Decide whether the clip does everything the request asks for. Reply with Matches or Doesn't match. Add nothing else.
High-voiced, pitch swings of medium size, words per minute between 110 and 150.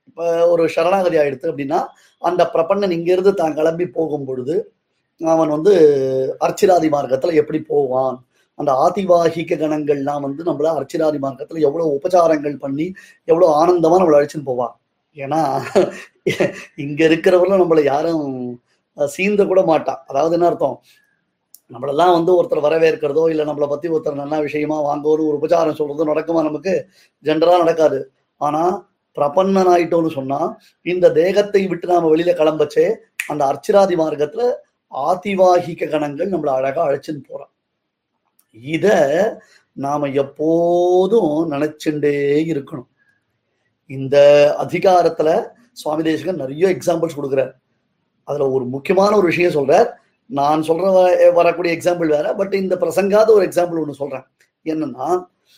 Doesn't match